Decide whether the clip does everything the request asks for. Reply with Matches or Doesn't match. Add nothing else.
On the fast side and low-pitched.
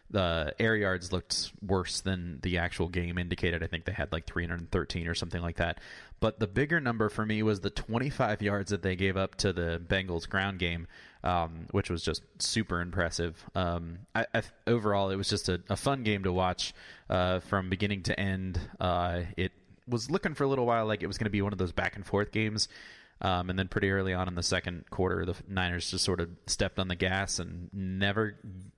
Matches